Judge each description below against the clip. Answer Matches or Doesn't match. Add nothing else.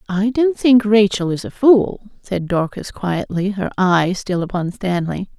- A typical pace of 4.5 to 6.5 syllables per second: Doesn't match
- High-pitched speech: Matches